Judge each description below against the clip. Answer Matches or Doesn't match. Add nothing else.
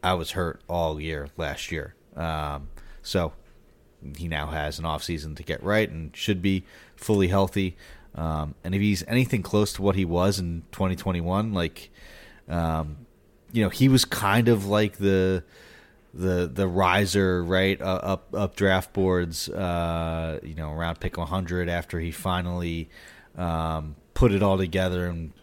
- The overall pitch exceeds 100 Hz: Doesn't match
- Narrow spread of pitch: Doesn't match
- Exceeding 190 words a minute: Doesn't match